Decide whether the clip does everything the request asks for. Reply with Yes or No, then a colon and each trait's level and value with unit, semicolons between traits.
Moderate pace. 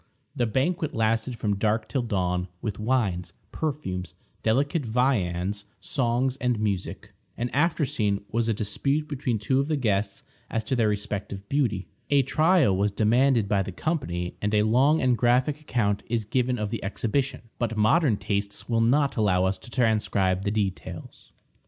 Yes: average, 165 wpm